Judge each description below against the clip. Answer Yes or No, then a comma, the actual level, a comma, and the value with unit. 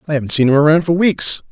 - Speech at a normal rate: No, fast, 275 wpm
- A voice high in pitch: No, medium, 155 Hz